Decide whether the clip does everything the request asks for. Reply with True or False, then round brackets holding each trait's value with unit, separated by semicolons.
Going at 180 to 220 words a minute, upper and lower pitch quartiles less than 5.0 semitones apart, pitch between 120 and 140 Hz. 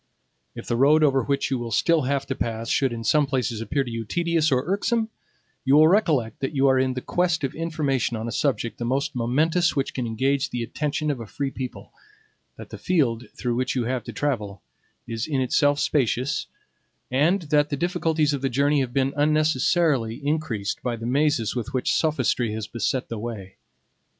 True (200 wpm; 4.2 semitones; 135 Hz)